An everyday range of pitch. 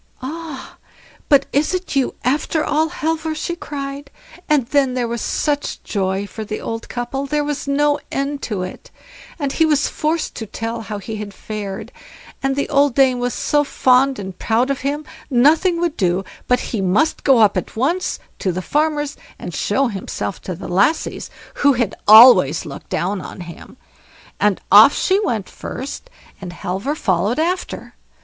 No: wide, 5.9 semitones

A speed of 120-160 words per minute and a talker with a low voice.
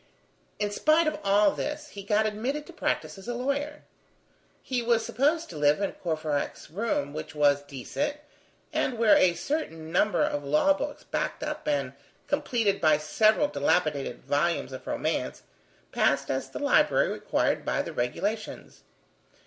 No: average, 155 wpm; high, 205 Hz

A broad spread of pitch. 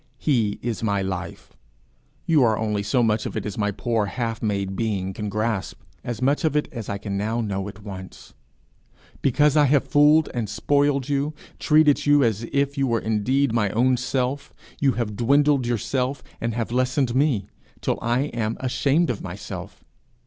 No: average, 4.7 semitones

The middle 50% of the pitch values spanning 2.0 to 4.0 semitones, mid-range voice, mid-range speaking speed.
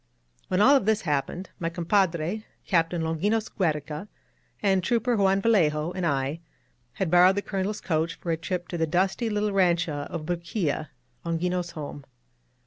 Yes: average, 3.4 semitones; medium, 175 Hz; average, 155 wpm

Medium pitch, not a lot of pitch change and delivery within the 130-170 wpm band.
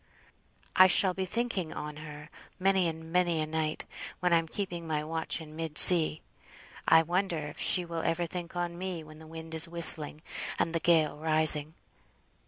No: medium, 165 Hz; narrow, 2.1 semitones; average, 180 wpm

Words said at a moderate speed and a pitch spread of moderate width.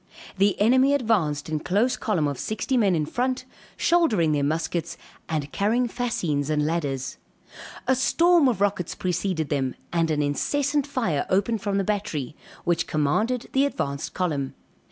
No: average, 155 wpm; wide, 8.1 semitones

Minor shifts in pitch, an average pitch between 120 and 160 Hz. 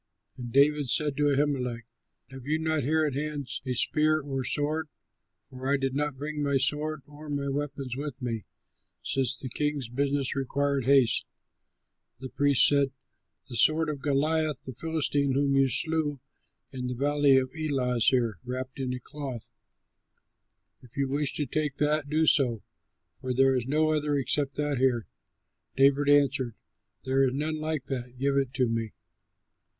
Yes: narrow, 2.2 semitones; medium, 140 Hz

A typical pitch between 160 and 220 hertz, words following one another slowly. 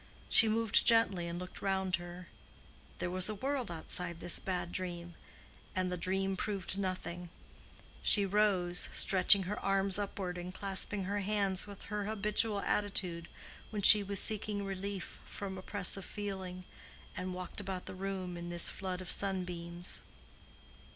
No: high, 190 Hz; average, 145 wpm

